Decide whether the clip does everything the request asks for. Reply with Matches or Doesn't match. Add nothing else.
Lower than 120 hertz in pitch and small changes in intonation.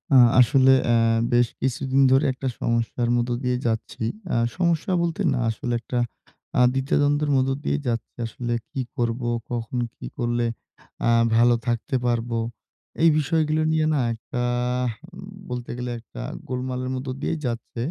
Doesn't match